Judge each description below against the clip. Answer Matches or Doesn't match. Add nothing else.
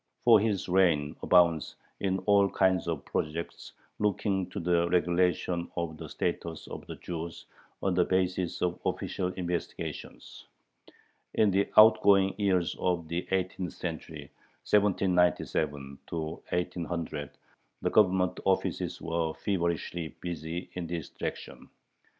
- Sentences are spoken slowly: Matches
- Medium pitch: Doesn't match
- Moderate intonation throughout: Doesn't match